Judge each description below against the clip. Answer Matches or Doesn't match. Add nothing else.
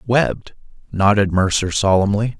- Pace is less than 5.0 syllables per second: Matches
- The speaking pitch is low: Matches